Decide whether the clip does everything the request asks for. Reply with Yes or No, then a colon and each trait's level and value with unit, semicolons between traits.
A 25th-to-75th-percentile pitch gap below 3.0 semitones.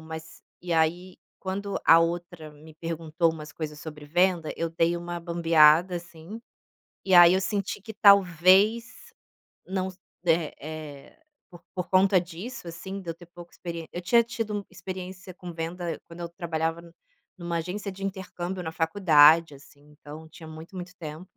Yes: narrow, 2.6 semitones